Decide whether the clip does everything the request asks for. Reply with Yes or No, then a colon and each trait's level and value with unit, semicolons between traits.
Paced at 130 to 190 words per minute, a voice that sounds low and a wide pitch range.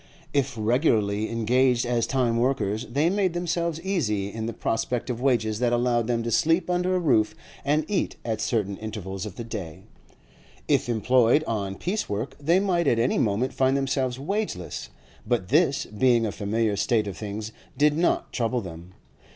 No: average, 175 wpm; low, 120 Hz; average, 4.6 semitones